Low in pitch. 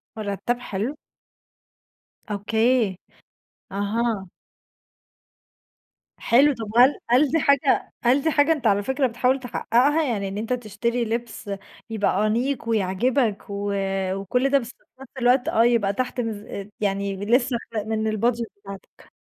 No: high, 230 Hz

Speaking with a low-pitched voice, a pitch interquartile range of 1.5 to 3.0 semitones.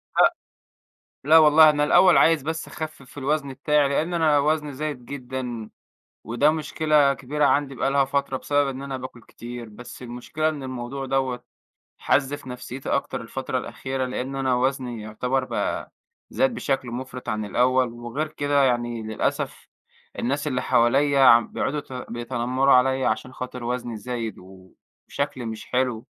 Yes: low, 130 Hz; average, 2.7 semitones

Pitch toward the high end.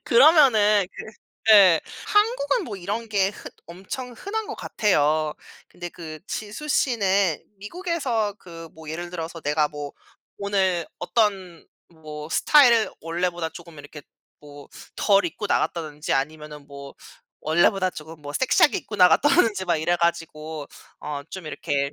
No: medium, 175 Hz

